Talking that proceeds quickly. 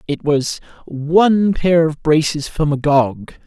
No: average, 140 wpm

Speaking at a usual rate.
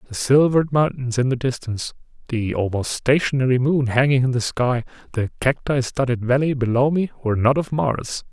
Yes: average, 175 wpm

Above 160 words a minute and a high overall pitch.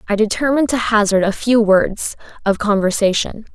No: average, 150 wpm; high, 215 Hz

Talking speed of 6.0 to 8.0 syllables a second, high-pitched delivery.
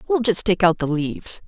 No: 5.5 syllables/s; high, 195 Hz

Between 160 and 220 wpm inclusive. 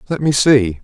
Yes: fast, 215 wpm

